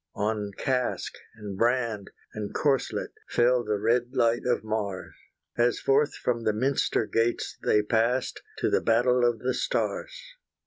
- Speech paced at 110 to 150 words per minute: Yes, average, 145 wpm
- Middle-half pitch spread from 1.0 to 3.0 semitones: Yes, average, 2.7 semitones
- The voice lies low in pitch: Yes, low, 115 Hz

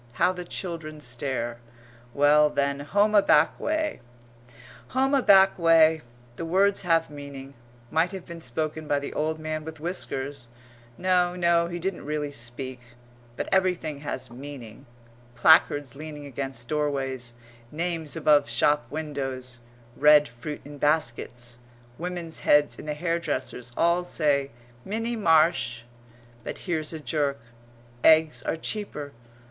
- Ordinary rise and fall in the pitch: Yes, average, 3.5 semitones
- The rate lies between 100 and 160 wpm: Yes, slow, 135 wpm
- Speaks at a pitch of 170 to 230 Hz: No, medium, 150 Hz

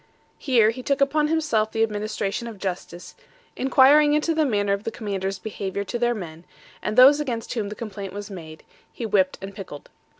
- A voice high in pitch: Yes, high, 215 Hz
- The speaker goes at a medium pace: Yes, average, 180 wpm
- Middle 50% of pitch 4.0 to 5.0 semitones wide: Yes, average, 4.6 semitones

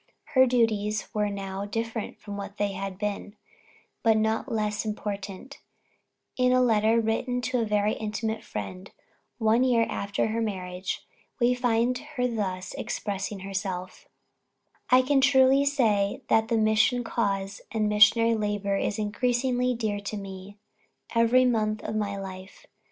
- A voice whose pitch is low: No, high, 215 Hz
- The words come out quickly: No, average, 145 wpm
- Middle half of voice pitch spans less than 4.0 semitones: Yes, average, 2.7 semitones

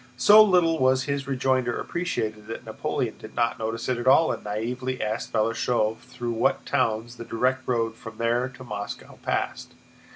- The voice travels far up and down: No, narrow, 2.4 semitones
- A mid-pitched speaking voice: No, low, 120 Hz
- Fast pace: No, average, 170 wpm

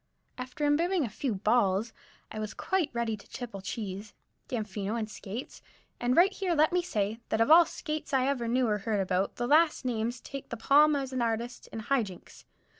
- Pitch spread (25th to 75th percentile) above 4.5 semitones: Yes, average, 5.0 semitones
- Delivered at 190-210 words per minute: Yes, average, 200 wpm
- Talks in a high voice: Yes, high, 240 Hz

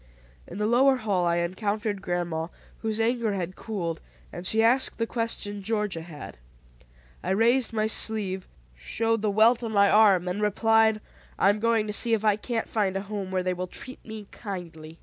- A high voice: Yes, high, 210 Hz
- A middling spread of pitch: Yes, average, 3.3 semitones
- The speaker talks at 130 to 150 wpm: No, average, 190 wpm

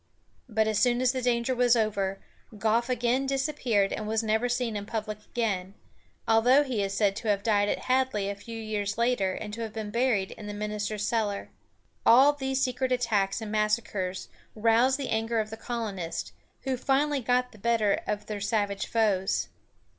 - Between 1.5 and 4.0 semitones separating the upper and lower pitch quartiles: Yes, average, 3.0 semitones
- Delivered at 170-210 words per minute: Yes, average, 185 wpm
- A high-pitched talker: Yes, high, 220 Hz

